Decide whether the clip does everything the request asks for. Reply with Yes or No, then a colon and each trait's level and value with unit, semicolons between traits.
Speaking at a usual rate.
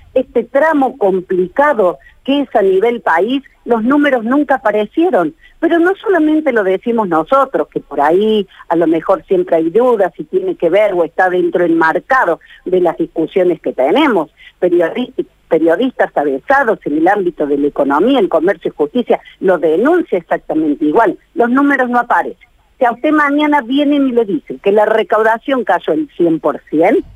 Yes: average, 170 wpm